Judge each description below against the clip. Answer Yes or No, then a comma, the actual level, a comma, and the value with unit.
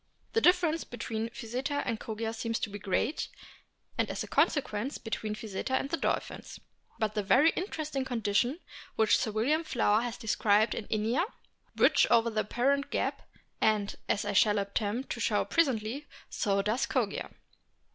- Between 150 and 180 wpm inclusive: Yes, average, 160 wpm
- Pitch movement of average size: Yes, average, 4.3 semitones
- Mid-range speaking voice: No, high, 230 Hz